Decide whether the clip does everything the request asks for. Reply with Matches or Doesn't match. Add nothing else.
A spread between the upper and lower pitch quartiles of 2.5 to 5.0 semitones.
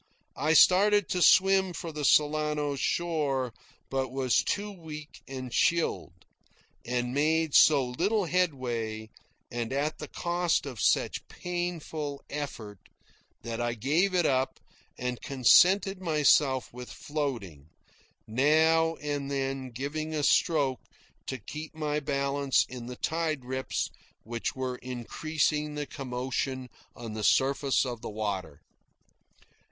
Matches